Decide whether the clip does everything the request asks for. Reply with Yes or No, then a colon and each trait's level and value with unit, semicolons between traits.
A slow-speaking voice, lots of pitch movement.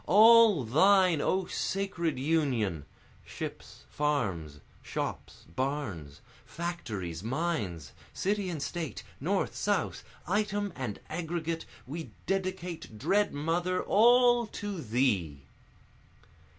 Yes: slow, 95 wpm; wide, 8.1 semitones